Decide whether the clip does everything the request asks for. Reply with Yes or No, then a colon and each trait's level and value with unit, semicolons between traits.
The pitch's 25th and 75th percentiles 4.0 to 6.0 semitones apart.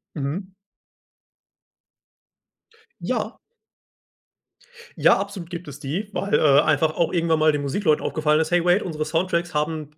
No: average, 2.8 semitones